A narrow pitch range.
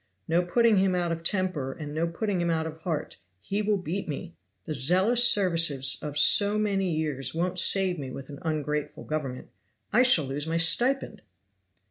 No: average, 4.4 semitones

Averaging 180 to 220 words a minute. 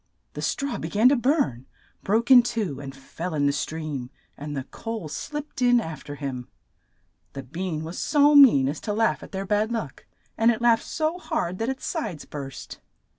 Yes: average, 195 wpm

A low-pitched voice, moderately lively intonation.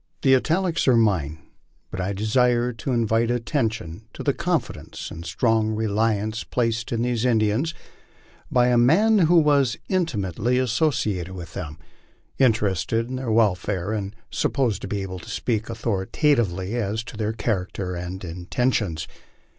Yes: low, 110 Hz; average, 4.1 semitones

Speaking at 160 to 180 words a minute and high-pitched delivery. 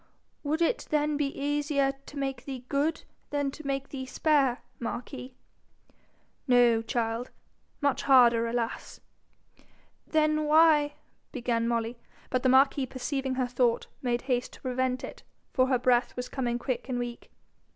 No: average, 150 wpm; very high, 260 Hz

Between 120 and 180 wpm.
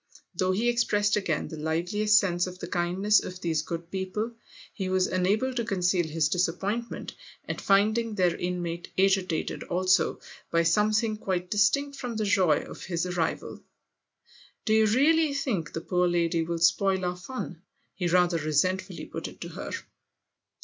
Yes: average, 165 wpm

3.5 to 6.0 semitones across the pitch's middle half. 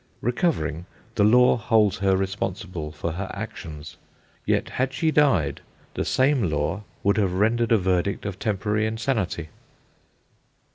Yes: average, 4.6 semitones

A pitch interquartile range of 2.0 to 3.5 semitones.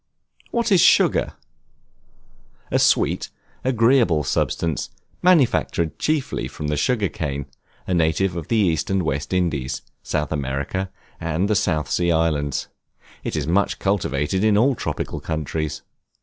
No: average, 5.2 semitones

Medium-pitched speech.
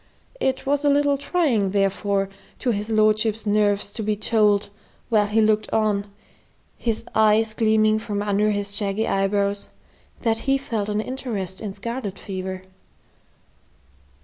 No: high, 215 Hz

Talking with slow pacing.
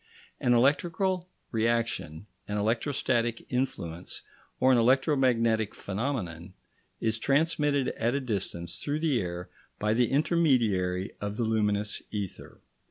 Yes: slow, 115 wpm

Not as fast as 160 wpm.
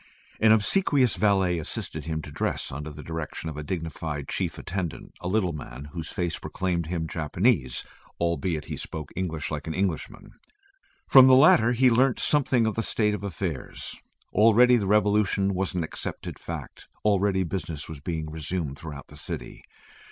No: average, 165 wpm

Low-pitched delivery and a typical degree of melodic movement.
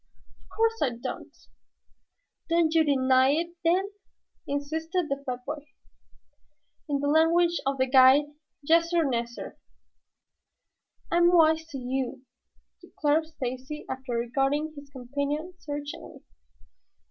No: very high, 290 Hz; average, 3.7 semitones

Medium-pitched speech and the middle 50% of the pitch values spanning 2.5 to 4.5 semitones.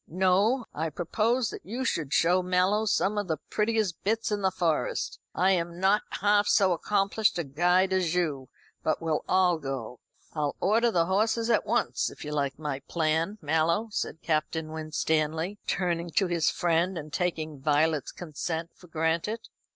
Yes: medium, 175 Hz; average, 4.1 semitones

